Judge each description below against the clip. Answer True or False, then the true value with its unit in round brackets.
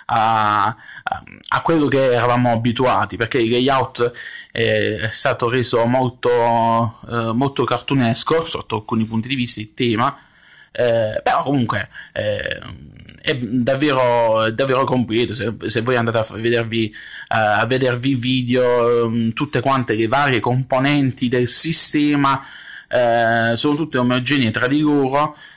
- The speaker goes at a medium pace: True (130 wpm)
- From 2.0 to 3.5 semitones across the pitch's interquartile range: True (2.7 semitones)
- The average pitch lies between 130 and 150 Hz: False (120 Hz)